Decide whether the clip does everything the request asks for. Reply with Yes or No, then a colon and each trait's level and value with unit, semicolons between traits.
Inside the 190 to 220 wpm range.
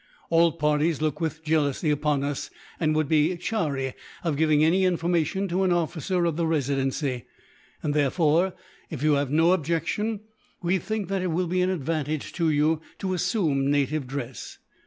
No: average, 170 wpm